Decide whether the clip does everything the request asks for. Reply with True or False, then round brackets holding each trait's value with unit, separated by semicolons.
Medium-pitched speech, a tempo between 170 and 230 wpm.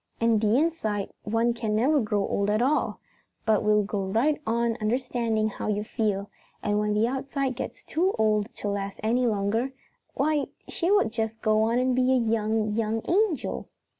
False (225 Hz; 175 wpm)